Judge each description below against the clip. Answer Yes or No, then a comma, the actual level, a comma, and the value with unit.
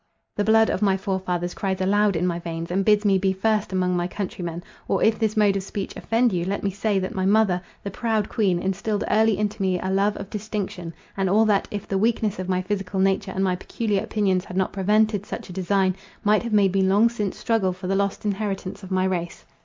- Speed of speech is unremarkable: No, fast, 235 wpm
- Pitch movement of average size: No, narrow, 2.1 semitones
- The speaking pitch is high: Yes, high, 195 Hz